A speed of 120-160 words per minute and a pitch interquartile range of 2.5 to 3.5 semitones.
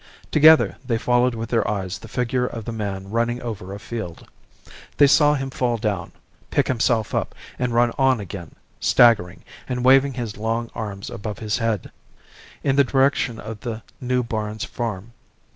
No: average, 170 wpm; average, 3.0 semitones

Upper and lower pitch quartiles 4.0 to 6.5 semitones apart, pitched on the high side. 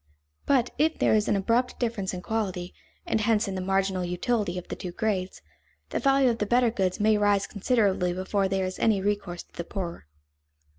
No: average, 3.2 semitones; high, 200 Hz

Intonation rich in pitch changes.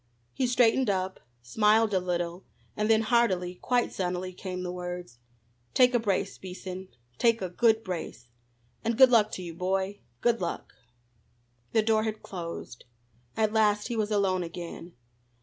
No: average, 3.7 semitones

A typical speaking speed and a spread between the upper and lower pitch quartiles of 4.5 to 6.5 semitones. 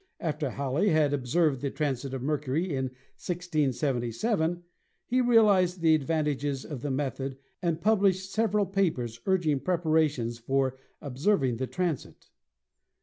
No: slow, 130 wpm; average, 5.1 semitones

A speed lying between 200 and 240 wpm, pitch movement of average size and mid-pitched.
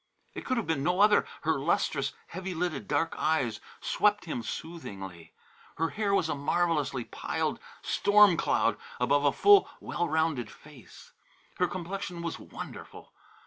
No: average, 145 wpm; average, 4.7 semitones; medium, 165 Hz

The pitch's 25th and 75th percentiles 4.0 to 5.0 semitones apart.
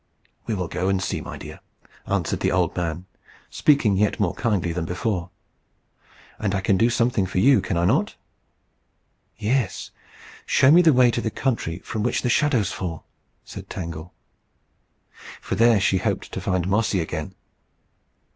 Yes: average, 4.6 semitones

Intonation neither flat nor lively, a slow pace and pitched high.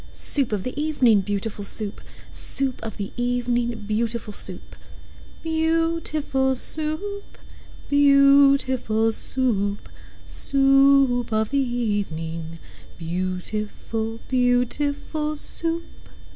Yes: average, 4.6 semitones; slow, 110 wpm; high, 245 Hz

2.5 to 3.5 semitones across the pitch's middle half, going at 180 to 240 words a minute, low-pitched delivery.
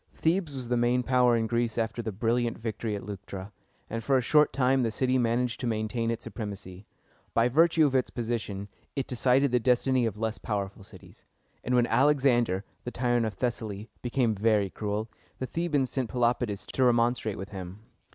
Yes: average, 2.8 semitones; average, 190 wpm; low, 120 Hz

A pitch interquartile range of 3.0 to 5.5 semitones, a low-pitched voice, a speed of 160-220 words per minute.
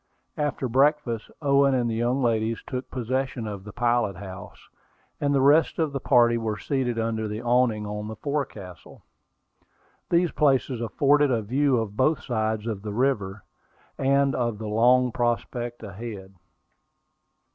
No: average, 3.7 semitones; low, 120 Hz; average, 150 wpm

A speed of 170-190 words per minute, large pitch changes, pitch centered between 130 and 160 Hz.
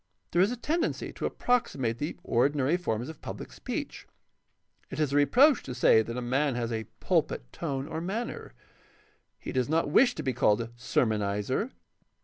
Yes: average, 180 wpm; wide, 6.7 semitones; low, 135 Hz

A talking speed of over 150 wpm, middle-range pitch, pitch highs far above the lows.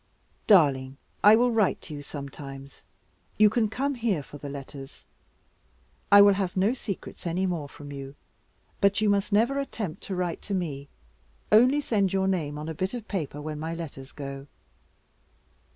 Yes: average, 170 wpm; medium, 180 Hz; wide, 6.3 semitones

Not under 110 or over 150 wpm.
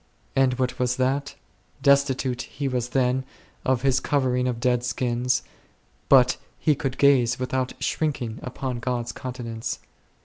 Yes: average, 140 wpm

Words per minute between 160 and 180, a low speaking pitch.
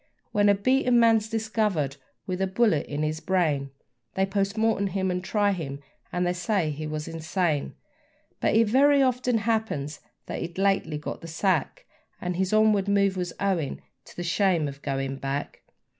No: average, 175 wpm; high, 190 Hz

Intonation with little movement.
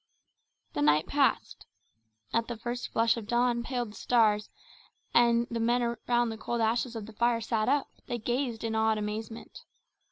Yes: narrow, 1.5 semitones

